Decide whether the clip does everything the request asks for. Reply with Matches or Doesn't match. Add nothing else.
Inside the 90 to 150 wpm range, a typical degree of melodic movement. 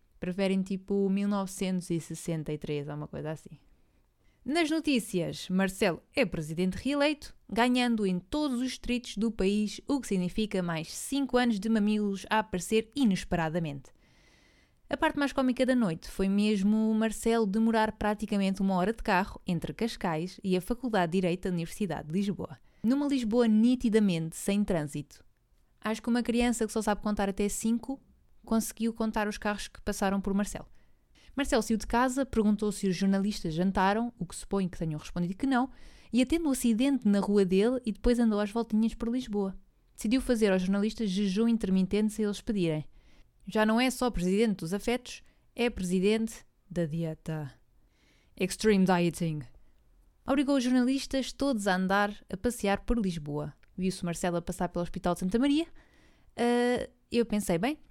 Doesn't match